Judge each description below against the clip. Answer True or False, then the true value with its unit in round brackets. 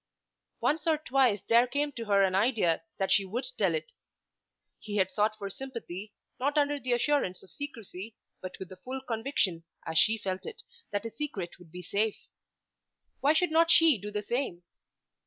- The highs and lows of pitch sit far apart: True (6.3 semitones)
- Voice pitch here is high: True (225 Hz)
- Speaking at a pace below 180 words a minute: False (185 wpm)